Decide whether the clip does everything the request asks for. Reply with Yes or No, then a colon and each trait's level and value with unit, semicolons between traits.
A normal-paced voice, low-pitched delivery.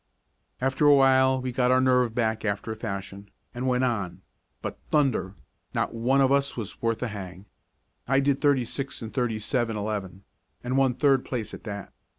Yes: average, 185 wpm; low, 120 Hz